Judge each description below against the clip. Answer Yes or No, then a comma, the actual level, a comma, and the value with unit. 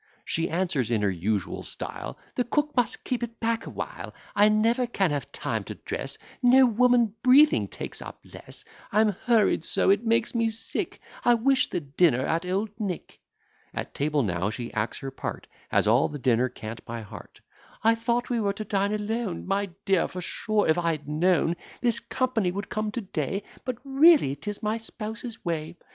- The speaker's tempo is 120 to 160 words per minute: No, average, 190 wpm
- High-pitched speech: Yes, high, 205 Hz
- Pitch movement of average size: No, wide, 7.1 semitones